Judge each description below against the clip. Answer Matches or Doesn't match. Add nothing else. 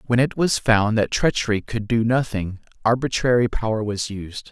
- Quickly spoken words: Doesn't match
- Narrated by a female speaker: Doesn't match